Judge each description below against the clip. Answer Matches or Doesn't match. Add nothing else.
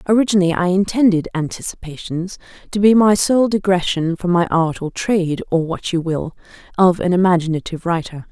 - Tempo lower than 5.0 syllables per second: Doesn't match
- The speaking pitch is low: Doesn't match